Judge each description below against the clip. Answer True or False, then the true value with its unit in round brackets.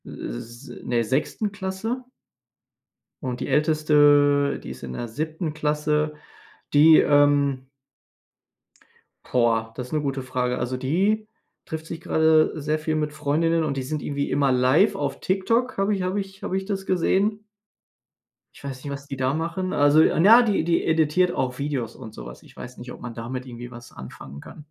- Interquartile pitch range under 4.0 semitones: False (4.4 semitones)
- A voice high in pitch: False (150 Hz)